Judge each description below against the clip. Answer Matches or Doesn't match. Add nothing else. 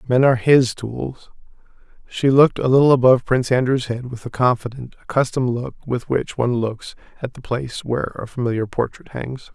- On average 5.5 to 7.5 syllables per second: Matches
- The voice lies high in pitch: Doesn't match